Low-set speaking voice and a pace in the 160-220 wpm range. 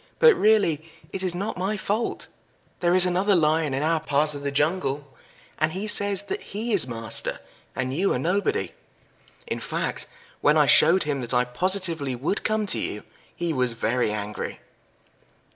No: medium, 165 Hz; average, 175 wpm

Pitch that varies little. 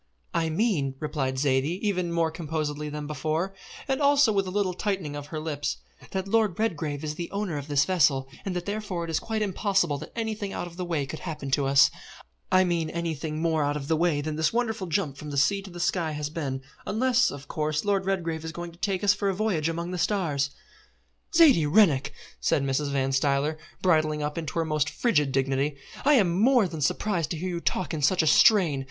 No: average, 4.7 semitones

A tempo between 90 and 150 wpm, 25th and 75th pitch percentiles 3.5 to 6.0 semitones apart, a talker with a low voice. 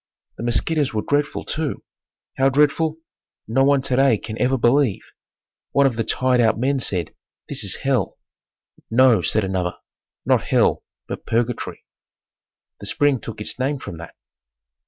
Yes: average, 145 wpm; average, 3.8 semitones; low, 125 Hz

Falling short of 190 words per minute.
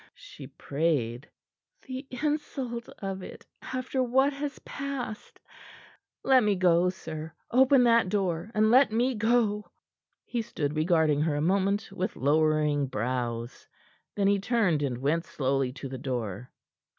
Yes: average, 140 wpm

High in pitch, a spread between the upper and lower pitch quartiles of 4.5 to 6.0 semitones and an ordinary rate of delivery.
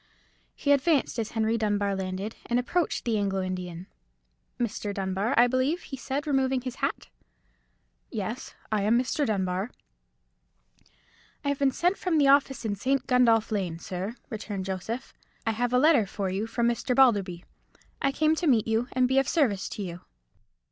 Yes: high, 230 Hz; average, 5.0 semitones; average, 175 wpm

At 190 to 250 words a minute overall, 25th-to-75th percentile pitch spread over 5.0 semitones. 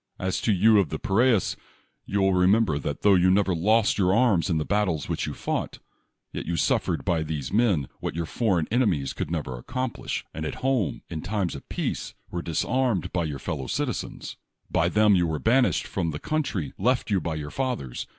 Yes: average, 200 wpm; wide, 5.5 semitones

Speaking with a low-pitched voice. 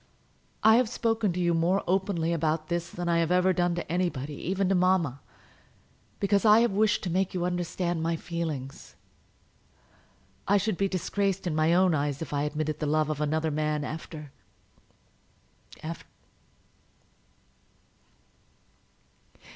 No: medium, 170 Hz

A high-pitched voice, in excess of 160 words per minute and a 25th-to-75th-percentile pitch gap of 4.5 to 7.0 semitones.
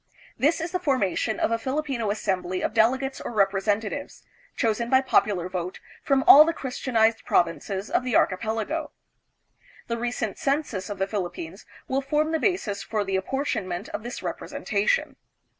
No: high, 225 Hz; average, 155 wpm; wide, 5.6 semitones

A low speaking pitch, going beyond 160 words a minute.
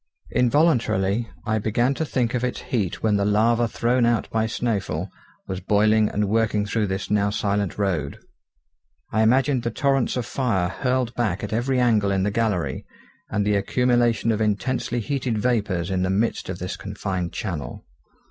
Yes: low, 110 Hz; average, 170 wpm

